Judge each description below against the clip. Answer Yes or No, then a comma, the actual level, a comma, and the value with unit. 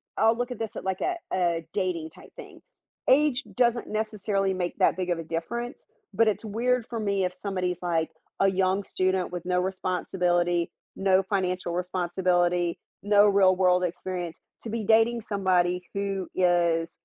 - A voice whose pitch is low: No, medium, 185 Hz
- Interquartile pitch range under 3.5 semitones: Yes, average, 2.9 semitones